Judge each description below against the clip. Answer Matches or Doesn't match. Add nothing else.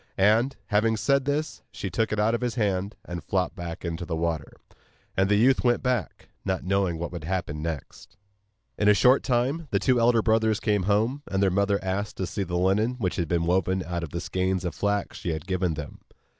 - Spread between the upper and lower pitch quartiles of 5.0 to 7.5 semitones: Doesn't match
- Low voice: Matches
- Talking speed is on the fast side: Matches